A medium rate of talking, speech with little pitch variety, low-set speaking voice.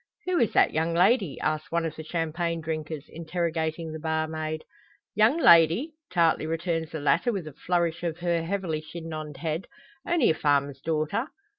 No: average, 165 wpm; narrow, 1.8 semitones; medium, 165 Hz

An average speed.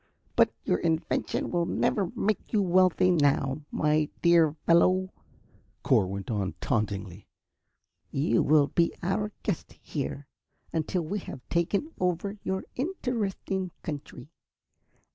No: slow, 120 wpm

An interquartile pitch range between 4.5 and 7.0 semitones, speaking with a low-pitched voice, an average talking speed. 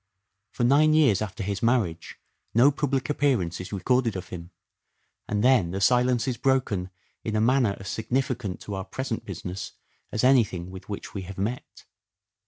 Yes: average, 5.1 semitones; low, 110 Hz; average, 170 wpm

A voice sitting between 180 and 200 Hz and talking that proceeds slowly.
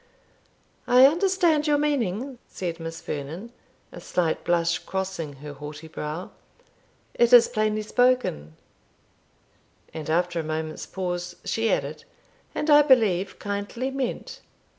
Yes: high, 190 Hz; slow, 120 wpm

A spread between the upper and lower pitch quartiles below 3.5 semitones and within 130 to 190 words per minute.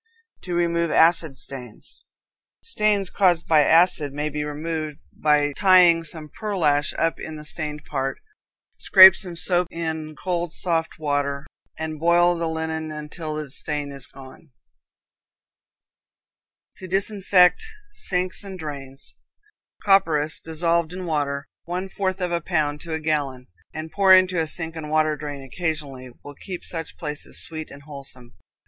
Yes: average, 2.9 semitones; average, 145 wpm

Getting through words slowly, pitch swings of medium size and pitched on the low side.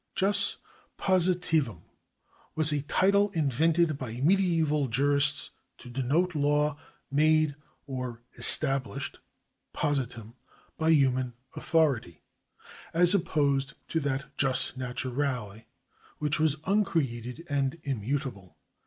No: slow, 95 wpm; average, 3.7 semitones; medium, 145 Hz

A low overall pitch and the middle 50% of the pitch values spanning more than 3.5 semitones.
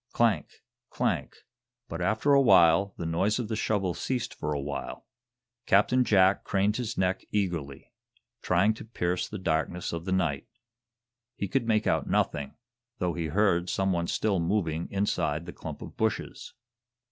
Yes: very low, 95 Hz; average, 4.2 semitones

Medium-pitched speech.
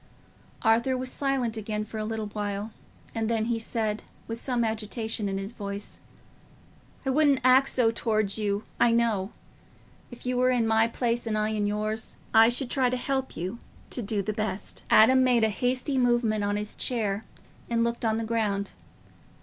No: high, 225 Hz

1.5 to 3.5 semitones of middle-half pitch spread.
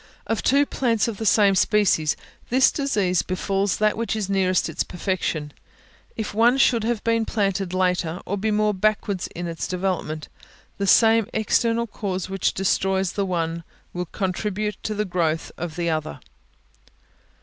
Yes: average, 3.1 semitones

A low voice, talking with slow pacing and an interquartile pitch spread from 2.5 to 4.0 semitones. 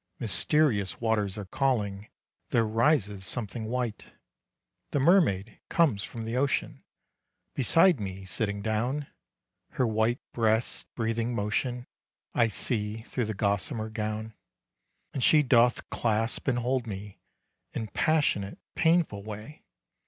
Yes: low, 115 Hz; slow, 120 wpm; average, 3.3 semitones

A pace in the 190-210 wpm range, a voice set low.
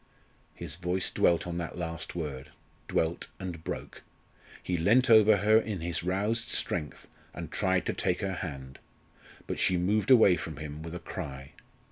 No: average, 165 wpm; very low, 90 Hz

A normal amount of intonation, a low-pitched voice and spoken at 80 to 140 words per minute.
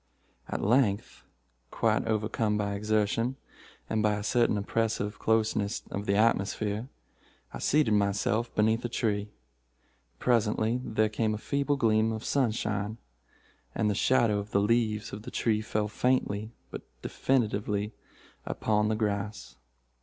No: narrow, 1.6 semitones; low, 110 Hz; slow, 135 wpm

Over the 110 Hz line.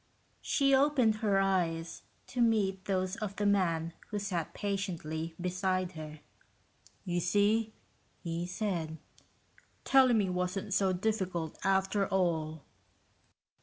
Yes: high, 190 Hz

